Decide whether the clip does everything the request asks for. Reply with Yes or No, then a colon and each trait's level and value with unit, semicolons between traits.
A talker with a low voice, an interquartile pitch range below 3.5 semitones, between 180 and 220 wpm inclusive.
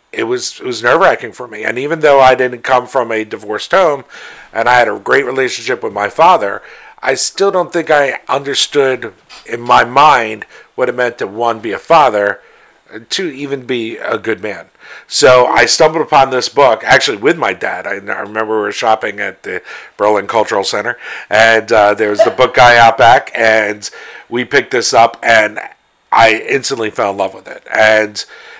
No: low, 125 Hz; average, 4.1 semitones; average, 195 wpm